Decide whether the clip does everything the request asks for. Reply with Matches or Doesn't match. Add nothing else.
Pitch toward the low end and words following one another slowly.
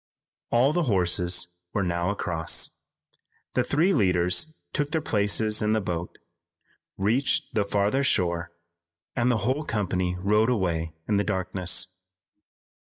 Matches